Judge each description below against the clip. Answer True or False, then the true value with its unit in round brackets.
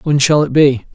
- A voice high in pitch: False (140 Hz)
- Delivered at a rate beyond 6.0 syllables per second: False (5.1 syllables/s)